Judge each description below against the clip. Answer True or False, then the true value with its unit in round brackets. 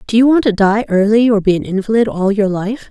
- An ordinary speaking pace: False (270 wpm)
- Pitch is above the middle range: True (210 Hz)